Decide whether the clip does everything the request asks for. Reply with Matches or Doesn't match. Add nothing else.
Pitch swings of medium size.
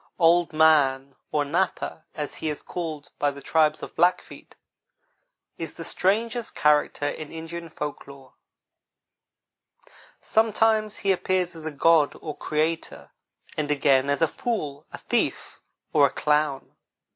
Matches